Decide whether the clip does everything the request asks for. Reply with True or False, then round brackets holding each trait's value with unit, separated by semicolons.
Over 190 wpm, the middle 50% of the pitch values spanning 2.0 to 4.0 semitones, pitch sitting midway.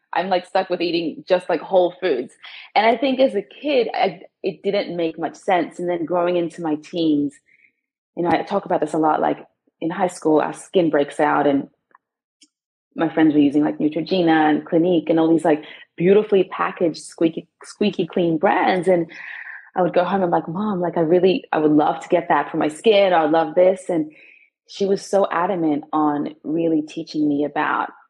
True (205 wpm; 3.0 semitones; 170 Hz)